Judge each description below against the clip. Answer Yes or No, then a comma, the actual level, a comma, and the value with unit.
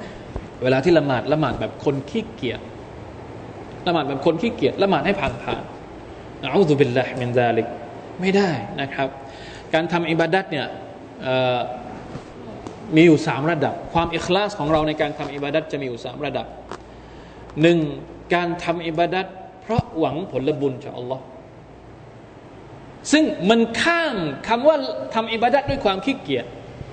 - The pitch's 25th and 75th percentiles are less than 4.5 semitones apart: No, average, 4.9 semitones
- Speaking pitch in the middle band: Yes, medium, 150 Hz